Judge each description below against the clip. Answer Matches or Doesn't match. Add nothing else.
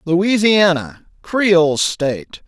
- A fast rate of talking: Doesn't match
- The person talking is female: Doesn't match